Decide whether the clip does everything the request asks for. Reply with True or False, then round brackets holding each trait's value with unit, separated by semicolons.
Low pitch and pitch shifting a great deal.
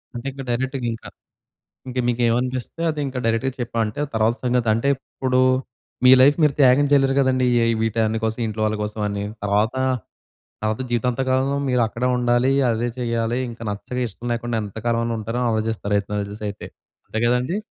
False (120 Hz; 2.5 semitones)